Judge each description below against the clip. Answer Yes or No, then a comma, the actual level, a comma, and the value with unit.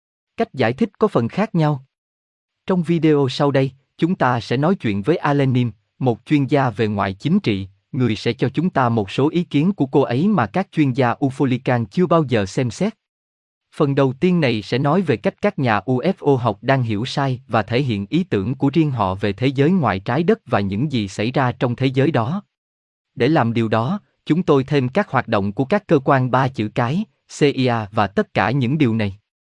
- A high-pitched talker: No, low, 135 Hz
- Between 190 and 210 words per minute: No, average, 220 wpm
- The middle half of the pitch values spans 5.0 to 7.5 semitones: Yes, wide, 5.4 semitones